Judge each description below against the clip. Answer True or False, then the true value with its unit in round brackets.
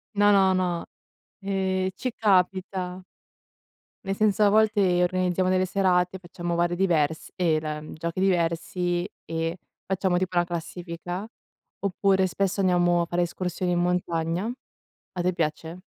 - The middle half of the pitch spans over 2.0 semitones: False (1.7 semitones)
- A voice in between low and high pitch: True (180 Hz)